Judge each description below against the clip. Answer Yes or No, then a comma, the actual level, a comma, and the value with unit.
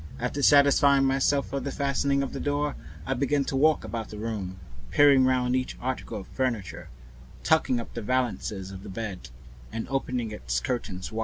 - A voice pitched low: Yes, low, 130 Hz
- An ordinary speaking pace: Yes, average, 180 wpm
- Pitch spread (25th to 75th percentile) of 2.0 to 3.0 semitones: No, average, 4.1 semitones